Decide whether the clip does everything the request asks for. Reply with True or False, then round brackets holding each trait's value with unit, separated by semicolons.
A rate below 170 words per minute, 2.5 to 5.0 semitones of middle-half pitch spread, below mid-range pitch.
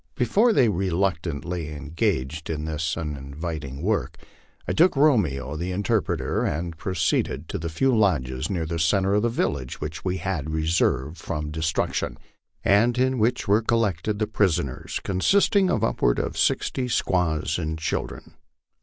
False (150 wpm; 5.5 semitones; 85 Hz)